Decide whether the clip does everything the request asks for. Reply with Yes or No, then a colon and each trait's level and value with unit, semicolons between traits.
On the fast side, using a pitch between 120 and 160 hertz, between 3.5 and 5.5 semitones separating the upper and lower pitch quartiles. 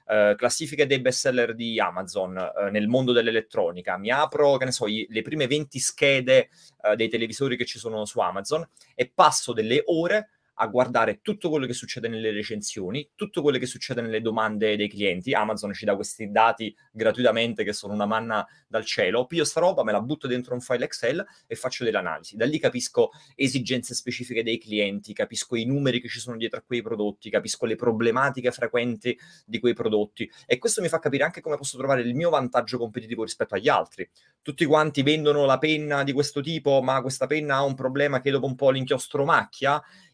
Yes: fast, 200 wpm; low, 125 Hz; average, 4.3 semitones